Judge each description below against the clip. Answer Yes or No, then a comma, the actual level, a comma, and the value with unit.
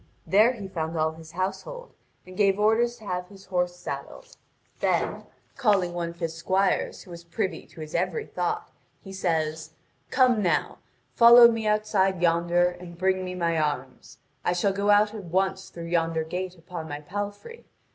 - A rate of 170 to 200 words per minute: Yes, average, 175 wpm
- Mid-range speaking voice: Yes, medium, 180 Hz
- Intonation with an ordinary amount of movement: Yes, average, 3.4 semitones